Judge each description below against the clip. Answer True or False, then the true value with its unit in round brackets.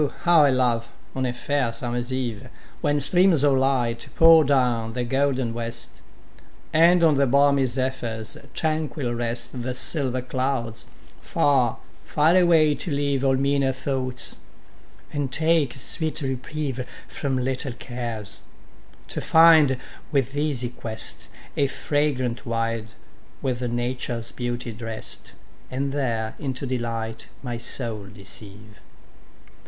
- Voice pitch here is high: False (130 Hz)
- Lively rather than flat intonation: False (3.2 semitones)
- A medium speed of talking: False (125 wpm)